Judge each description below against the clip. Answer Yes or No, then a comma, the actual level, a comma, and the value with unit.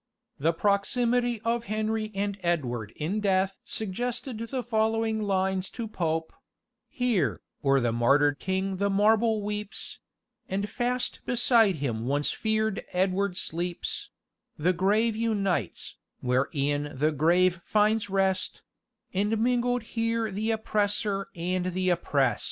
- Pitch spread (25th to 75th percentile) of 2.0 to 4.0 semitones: No, average, 4.4 semitones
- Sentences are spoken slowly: Yes, slow, 125 wpm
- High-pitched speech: Yes, high, 200 Hz